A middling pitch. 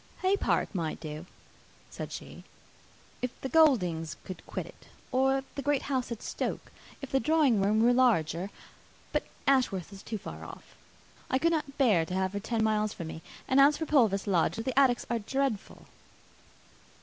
No: high, 235 Hz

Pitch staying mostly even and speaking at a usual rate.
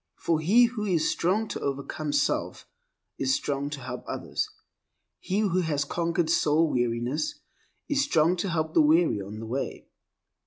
No: average, 4.1 semitones; average, 160 wpm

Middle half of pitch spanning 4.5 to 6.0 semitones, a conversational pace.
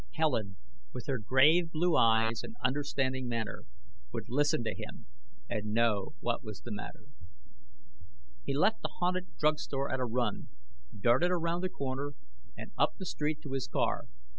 Yes: average, 4.8 semitones; average, 165 wpm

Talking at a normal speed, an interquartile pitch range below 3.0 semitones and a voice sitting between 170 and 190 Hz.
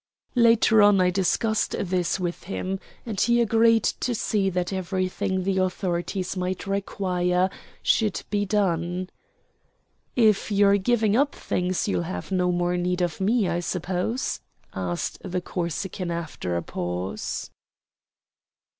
No: slow, 130 wpm; narrow, 2.6 semitones; medium, 185 Hz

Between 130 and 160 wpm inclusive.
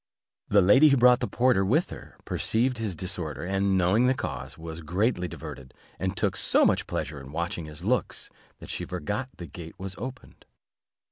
No: average, 185 wpm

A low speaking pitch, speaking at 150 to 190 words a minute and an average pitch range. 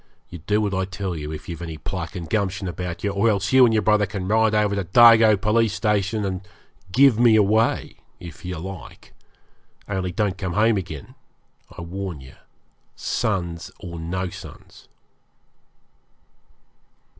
Yes: very low, 95 Hz; average, 160 wpm; average, 3.3 semitones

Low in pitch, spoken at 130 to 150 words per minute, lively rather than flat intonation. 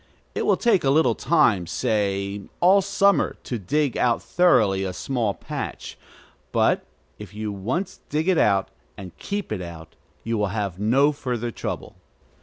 No: low, 115 Hz; average, 160 wpm; wide, 7.3 semitones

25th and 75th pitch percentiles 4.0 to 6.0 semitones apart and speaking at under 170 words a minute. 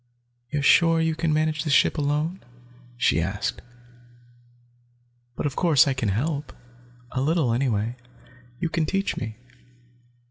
Yes: average, 4.8 semitones; slow, 135 wpm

